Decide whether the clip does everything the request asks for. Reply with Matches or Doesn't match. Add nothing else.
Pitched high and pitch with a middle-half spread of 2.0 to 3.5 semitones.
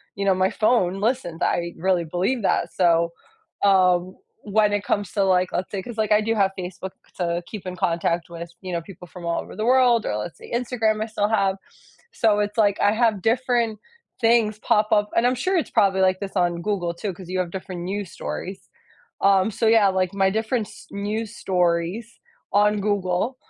Matches